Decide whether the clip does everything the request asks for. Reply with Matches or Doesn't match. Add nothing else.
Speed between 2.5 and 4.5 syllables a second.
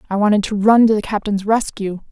Doesn't match